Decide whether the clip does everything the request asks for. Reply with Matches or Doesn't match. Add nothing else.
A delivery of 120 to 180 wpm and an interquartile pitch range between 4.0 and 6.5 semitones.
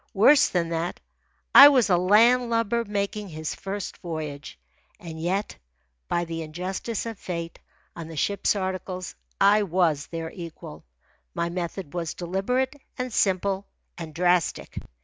Doesn't match